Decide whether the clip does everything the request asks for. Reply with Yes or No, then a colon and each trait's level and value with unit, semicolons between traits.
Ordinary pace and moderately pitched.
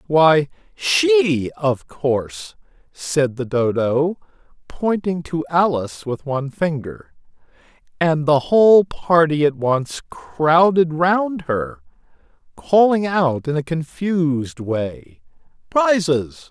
No: slow, 105 wpm; medium, 155 Hz